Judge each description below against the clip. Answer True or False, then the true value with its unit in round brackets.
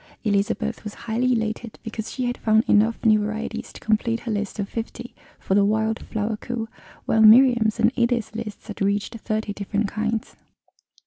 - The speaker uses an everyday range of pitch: False (1.5 semitones)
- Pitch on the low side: False (220 Hz)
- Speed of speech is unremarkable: True (175 wpm)